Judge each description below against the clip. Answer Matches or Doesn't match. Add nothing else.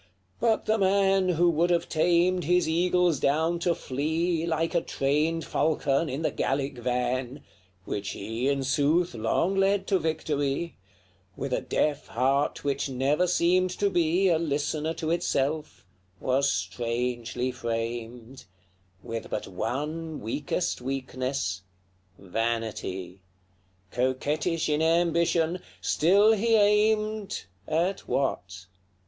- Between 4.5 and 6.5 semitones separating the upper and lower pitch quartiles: Matches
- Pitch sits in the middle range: Matches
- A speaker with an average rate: Doesn't match